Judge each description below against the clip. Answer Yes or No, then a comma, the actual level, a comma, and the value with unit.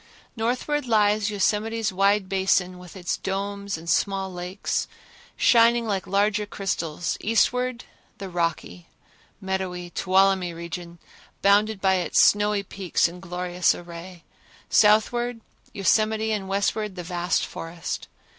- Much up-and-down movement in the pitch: No, average, 2.9 semitones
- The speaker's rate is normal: No, slow, 115 wpm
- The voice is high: Yes, high, 195 Hz